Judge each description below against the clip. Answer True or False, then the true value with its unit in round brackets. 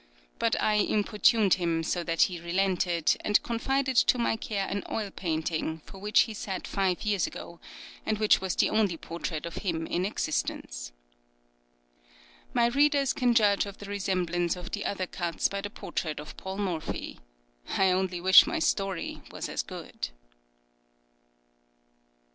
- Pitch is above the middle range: True (195 Hz)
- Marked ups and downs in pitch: False (3.5 semitones)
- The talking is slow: False (155 wpm)